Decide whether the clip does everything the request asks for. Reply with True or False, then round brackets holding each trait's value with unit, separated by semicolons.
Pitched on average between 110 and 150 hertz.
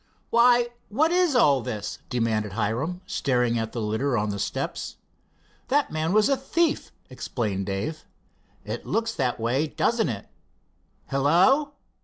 True (140 Hz)